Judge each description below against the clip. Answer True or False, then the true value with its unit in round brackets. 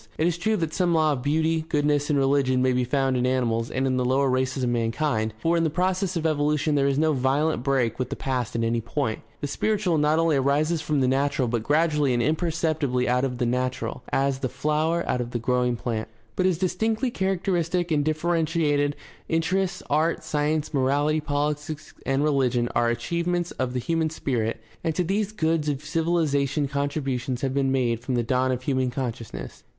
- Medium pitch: True (145 Hz)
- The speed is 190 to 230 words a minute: True (200 wpm)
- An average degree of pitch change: True (3.9 semitones)